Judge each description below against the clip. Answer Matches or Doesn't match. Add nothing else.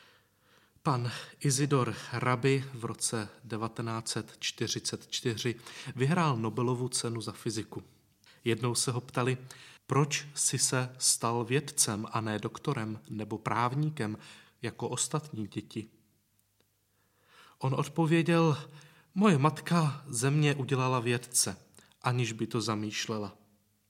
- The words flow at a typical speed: Doesn't match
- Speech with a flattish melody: Doesn't match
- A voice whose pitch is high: Doesn't match